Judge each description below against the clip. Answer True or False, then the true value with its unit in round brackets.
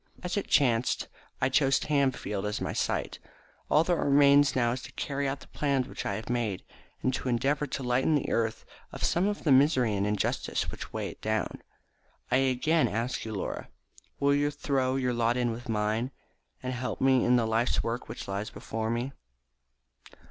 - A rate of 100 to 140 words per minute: False (190 wpm)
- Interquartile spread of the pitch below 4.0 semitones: True (3.5 semitones)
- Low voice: True (125 Hz)